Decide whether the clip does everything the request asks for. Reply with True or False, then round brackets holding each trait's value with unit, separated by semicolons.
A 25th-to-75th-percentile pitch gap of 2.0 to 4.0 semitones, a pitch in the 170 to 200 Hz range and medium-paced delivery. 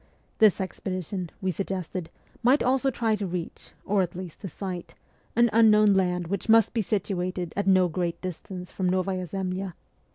True (2.5 semitones; 190 Hz; 170 wpm)